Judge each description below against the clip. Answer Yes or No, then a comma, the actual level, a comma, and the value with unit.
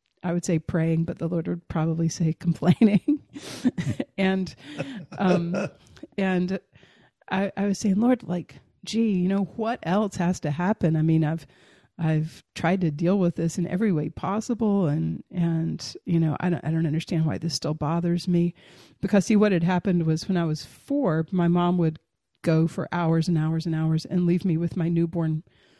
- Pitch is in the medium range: Yes, medium, 170 Hz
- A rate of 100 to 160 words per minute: No, average, 190 wpm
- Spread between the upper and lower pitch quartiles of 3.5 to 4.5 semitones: No, average, 2.8 semitones